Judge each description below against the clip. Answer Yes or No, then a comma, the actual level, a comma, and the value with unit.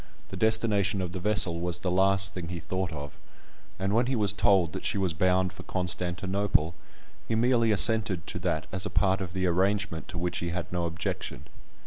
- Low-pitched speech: Yes, very low, 95 Hz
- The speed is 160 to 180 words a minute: No, average, 200 wpm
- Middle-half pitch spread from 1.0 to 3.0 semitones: Yes, narrow, 2.6 semitones